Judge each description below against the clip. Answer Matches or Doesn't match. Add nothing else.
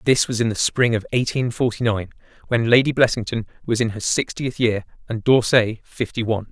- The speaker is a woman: Doesn't match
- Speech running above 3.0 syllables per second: Matches